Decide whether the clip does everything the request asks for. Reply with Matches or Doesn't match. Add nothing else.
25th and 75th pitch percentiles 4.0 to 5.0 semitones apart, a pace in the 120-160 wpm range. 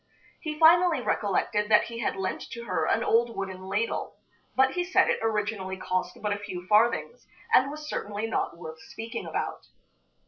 Doesn't match